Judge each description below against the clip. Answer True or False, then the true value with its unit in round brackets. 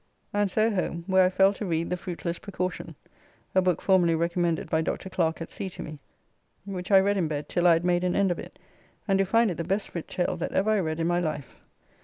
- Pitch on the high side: False (180 Hz)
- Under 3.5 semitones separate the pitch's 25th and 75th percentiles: True (2.4 semitones)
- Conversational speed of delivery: False (250 wpm)